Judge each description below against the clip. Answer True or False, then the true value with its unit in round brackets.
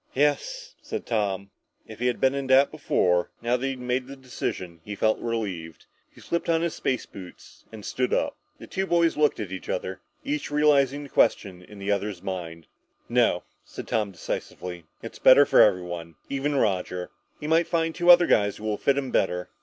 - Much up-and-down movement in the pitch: True (7.1 semitones)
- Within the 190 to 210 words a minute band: True (200 wpm)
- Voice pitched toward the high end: False (120 Hz)